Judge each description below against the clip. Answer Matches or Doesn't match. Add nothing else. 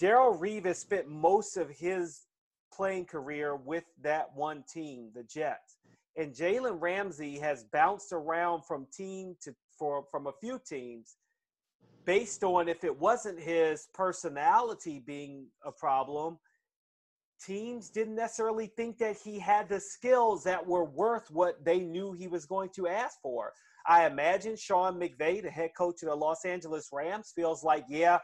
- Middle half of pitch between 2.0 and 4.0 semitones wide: Doesn't match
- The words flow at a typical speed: Matches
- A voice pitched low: Doesn't match